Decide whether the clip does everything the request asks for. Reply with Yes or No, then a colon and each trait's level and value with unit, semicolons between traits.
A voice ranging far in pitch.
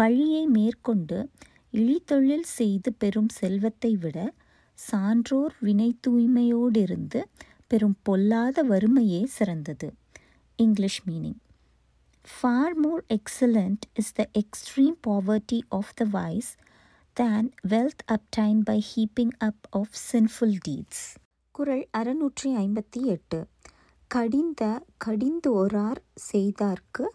No: average, 3.4 semitones